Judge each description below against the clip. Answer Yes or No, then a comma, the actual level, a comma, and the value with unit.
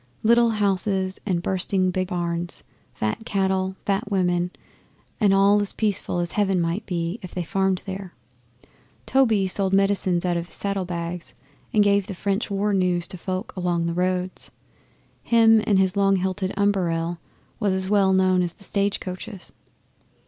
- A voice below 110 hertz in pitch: No, high, 190 Hz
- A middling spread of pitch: No, narrow, 2.0 semitones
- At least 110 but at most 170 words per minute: Yes, average, 160 wpm